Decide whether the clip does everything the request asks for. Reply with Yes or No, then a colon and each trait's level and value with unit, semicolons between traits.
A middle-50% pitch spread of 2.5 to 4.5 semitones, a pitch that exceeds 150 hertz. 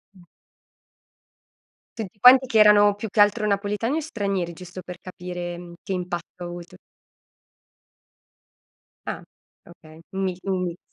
Yes: average, 2.9 semitones; medium, 185 Hz